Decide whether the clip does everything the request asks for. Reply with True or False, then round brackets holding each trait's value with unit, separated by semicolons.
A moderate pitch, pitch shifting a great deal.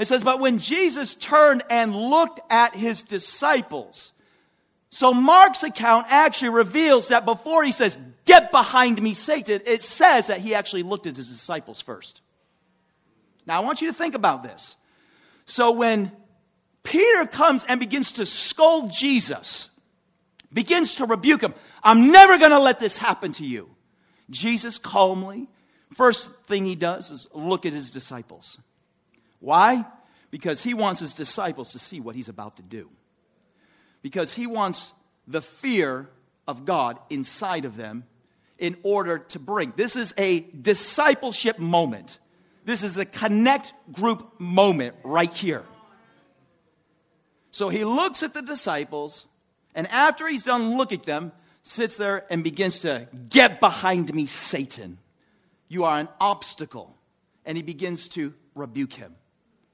False (210 Hz; 7.3 semitones)